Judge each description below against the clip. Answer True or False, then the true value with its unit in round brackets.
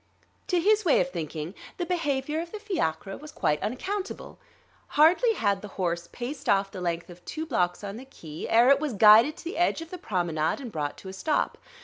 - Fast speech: True (215 wpm)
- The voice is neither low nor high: False (240 Hz)